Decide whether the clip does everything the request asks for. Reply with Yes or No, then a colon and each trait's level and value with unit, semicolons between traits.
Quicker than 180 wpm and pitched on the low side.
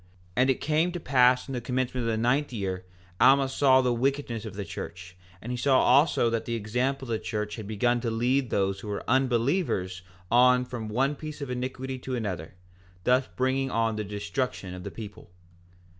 Yes: average, 200 wpm; low, 125 Hz